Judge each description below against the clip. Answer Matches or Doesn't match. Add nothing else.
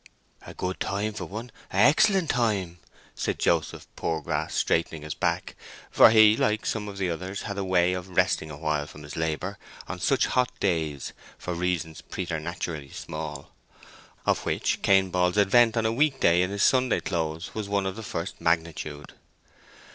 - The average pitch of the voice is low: Matches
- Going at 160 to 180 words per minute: Matches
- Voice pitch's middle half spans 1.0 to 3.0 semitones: Doesn't match